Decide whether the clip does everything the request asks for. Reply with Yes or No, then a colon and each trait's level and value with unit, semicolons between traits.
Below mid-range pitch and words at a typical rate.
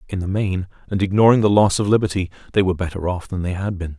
No: very low, 95 Hz; fast, 255 wpm